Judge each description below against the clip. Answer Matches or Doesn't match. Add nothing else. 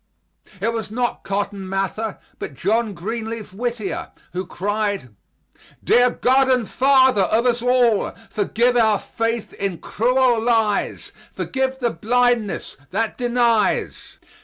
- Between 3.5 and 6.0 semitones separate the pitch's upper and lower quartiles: Doesn't match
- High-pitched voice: Matches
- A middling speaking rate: Doesn't match